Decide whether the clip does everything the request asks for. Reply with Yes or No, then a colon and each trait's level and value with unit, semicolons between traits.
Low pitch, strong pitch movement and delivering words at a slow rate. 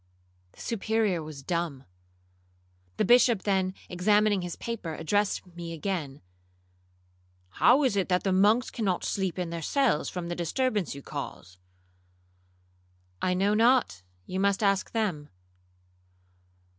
No: medium, 180 Hz; wide, 6.9 semitones; slow, 120 wpm